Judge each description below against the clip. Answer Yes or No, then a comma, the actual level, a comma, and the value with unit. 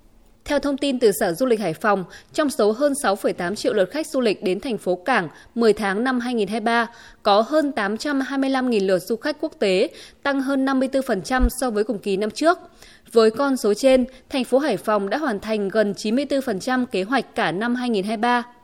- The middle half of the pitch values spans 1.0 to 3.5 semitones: No, average, 4.3 semitones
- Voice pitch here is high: Yes, high, 240 Hz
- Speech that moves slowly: No, average, 195 wpm